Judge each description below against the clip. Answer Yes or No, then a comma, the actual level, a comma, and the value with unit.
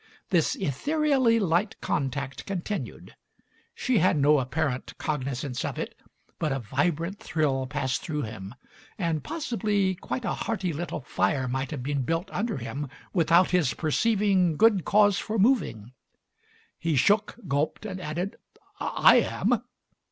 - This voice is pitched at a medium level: Yes, medium, 160 Hz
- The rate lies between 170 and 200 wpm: No, slow, 135 wpm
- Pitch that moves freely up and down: Yes, wide, 6.5 semitones